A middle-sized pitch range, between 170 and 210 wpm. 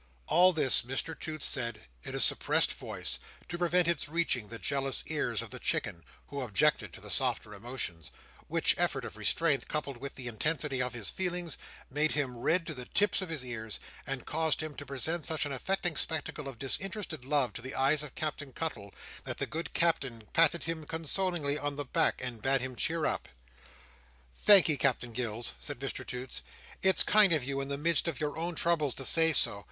Yes: average, 4.3 semitones; average, 200 wpm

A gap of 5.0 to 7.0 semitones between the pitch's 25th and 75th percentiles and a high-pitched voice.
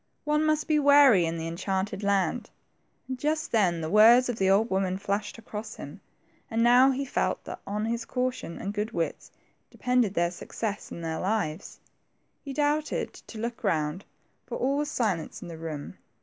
Yes: average, 5.3 semitones; high, 215 Hz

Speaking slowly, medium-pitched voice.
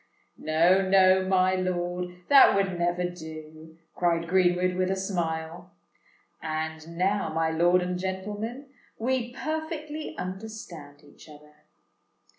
Yes: slow, 110 wpm; medium, 180 Hz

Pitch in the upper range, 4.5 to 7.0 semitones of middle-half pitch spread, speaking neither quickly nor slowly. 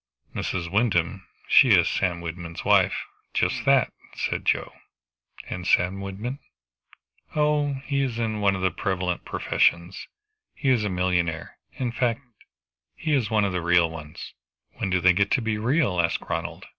No: very low, 95 Hz; average, 5.0 semitones; average, 155 wpm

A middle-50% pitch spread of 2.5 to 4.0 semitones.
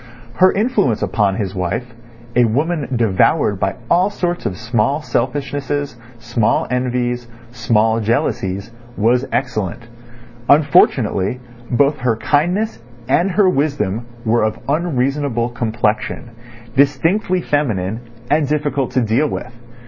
No: average, 4.7 semitones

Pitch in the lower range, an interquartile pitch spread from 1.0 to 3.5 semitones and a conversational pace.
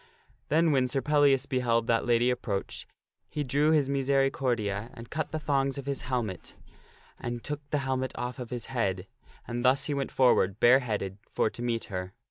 Yes: low, 125 Hz; average, 3.0 semitones; average, 185 wpm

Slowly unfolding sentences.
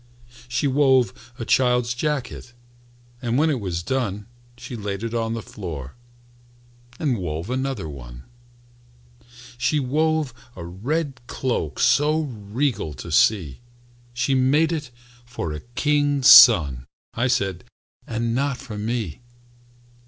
Yes: slow, 125 wpm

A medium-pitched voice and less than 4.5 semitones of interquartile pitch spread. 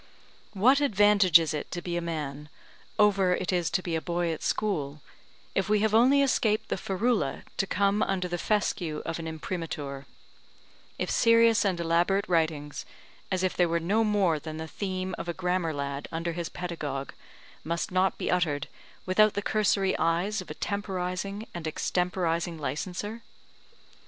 Yes: medium, 180 Hz; average, 3.7 semitones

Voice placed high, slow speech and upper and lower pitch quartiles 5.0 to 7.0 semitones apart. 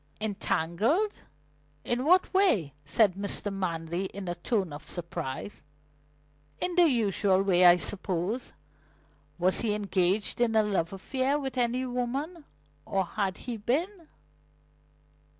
Yes: high, 205 Hz; slow, 125 wpm; wide, 5.6 semitones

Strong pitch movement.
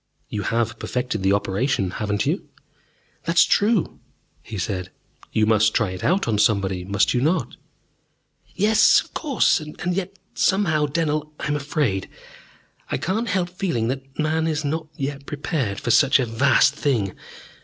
Yes: wide, 7.0 semitones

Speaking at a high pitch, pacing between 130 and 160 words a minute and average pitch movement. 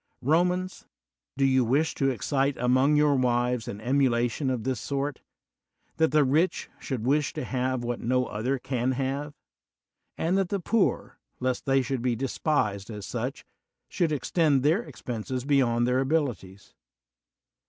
No: low, 130 Hz; average, 150 wpm; average, 3.1 semitones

